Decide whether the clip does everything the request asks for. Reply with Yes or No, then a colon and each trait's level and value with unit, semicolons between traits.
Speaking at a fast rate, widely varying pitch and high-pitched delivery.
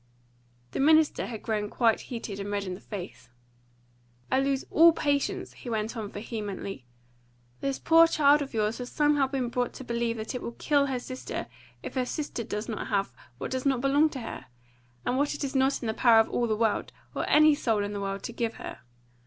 No: fast, 215 wpm; average, 4.3 semitones; high, 240 Hz